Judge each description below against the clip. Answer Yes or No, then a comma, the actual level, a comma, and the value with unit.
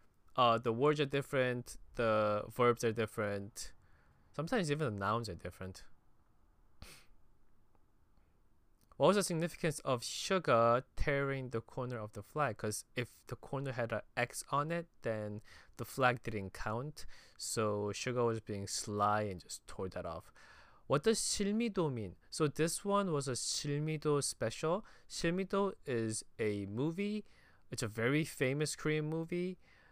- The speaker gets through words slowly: No, average, 145 wpm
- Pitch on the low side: Yes, low, 125 Hz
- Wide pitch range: Yes, wide, 6.2 semitones